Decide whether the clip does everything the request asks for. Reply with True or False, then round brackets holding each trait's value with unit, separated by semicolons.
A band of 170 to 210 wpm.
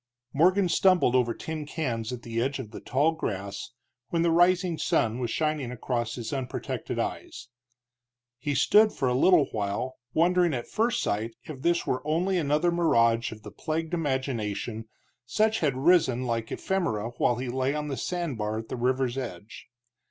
True (175 wpm)